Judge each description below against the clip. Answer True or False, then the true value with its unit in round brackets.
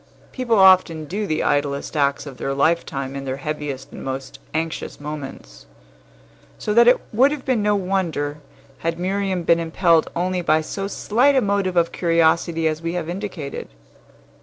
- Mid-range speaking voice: True (165 Hz)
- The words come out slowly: False (165 wpm)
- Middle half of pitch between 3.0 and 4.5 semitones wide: False (4.9 semitones)